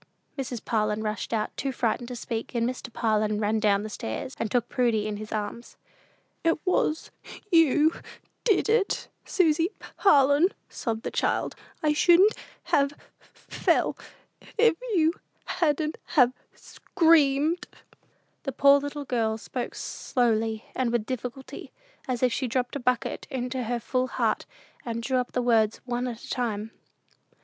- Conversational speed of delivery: Yes, average, 150 wpm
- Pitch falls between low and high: No, very high, 250 Hz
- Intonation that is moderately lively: Yes, average, 4.3 semitones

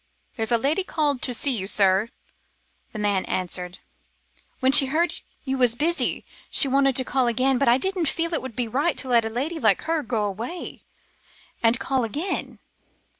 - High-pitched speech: Yes, very high, 255 Hz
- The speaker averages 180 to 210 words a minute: Yes, average, 185 wpm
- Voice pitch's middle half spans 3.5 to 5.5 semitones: Yes, average, 4.5 semitones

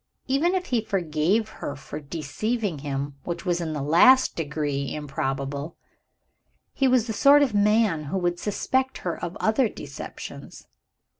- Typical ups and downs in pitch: No, wide, 7.3 semitones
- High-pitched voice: No, medium, 175 Hz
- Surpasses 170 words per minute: No, average, 150 wpm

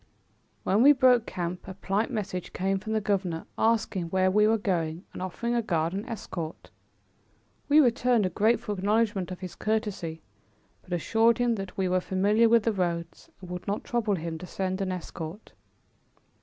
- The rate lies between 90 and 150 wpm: No, average, 180 wpm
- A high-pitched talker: Yes, high, 195 Hz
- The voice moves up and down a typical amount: Yes, average, 3.7 semitones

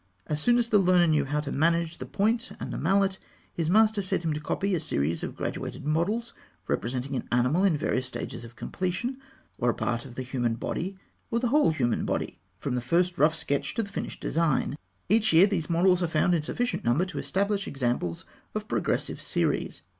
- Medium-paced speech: No, fast, 215 wpm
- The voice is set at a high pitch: No, medium, 165 Hz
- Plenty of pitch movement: Yes, wide, 6.4 semitones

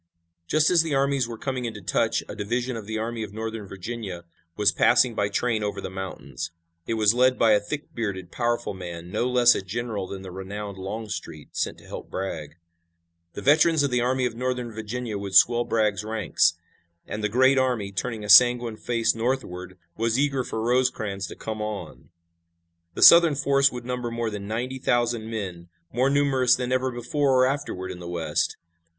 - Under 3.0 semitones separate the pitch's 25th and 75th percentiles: No, average, 3.8 semitones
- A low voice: Yes, low, 115 Hz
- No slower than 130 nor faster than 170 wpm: No, average, 190 wpm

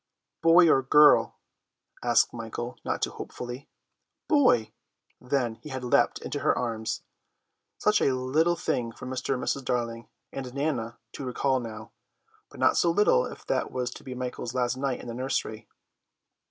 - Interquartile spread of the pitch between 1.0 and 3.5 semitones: Yes, average, 2.7 semitones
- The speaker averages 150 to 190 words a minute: Yes, average, 165 wpm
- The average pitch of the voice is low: Yes, low, 125 Hz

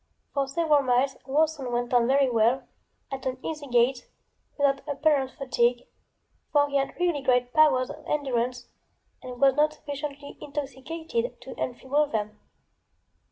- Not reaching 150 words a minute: Yes, average, 140 wpm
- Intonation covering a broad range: No, average, 2.9 semitones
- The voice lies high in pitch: Yes, very high, 275 Hz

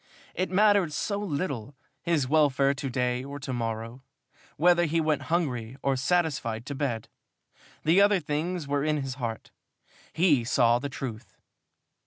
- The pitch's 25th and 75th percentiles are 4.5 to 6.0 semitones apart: Yes, average, 5.0 semitones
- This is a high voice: No, medium, 140 Hz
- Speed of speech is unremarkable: Yes, average, 155 wpm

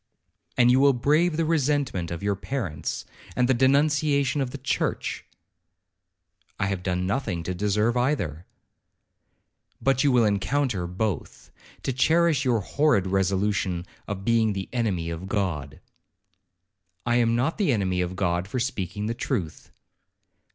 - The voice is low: Yes, low, 110 Hz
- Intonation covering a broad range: Yes, wide, 6.3 semitones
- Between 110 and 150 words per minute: Yes, average, 145 wpm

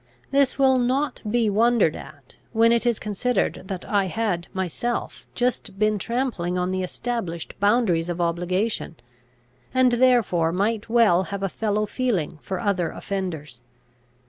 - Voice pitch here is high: Yes, high, 205 Hz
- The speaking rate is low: No, average, 145 wpm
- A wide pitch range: No, average, 5.0 semitones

